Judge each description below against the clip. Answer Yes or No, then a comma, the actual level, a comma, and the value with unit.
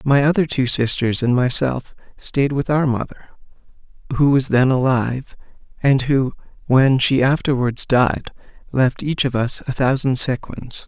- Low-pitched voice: Yes, low, 130 Hz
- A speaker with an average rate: Yes, average, 150 wpm